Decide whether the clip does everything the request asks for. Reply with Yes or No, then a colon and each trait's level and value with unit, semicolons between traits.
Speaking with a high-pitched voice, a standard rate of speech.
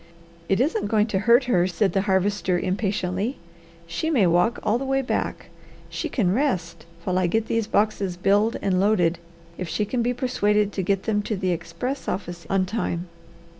Yes: high, 200 Hz; average, 185 wpm